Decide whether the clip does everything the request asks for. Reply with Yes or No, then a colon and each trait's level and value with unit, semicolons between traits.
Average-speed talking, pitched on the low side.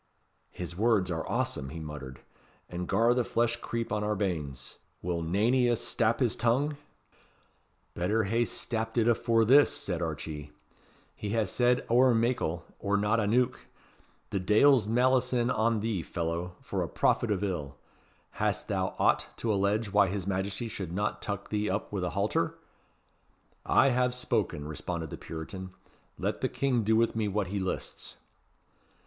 Yes: average, 165 wpm; low, 105 Hz